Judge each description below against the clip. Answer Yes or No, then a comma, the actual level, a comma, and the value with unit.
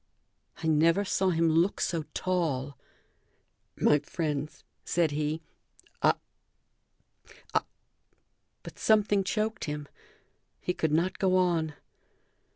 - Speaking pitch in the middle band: Yes, medium, 165 Hz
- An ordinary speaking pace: No, slow, 110 wpm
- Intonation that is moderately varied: Yes, average, 3.5 semitones